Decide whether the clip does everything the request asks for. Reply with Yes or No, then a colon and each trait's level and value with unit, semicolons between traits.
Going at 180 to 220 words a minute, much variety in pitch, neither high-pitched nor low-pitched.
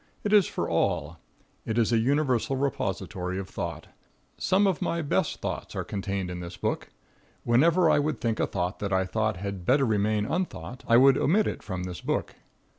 No: average, 190 wpm; wide, 7.1 semitones; low, 110 Hz